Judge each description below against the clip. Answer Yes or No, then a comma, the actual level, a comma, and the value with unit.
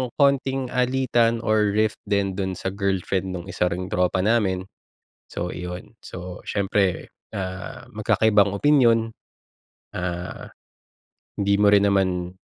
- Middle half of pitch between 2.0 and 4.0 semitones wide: Yes, average, 3.4 semitones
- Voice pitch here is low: Yes, low, 100 Hz